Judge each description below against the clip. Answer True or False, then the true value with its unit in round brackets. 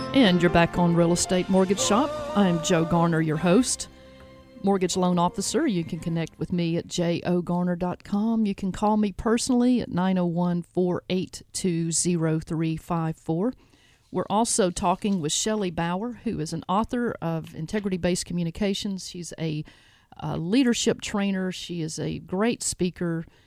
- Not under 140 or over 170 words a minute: True (145 wpm)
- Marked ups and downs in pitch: False (3.2 semitones)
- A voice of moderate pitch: True (180 Hz)